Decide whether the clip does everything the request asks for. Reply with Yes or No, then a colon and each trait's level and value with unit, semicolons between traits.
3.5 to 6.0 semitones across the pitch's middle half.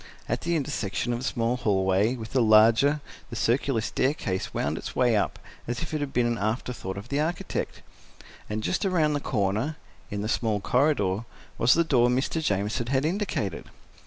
Yes: average, 5.2 semitones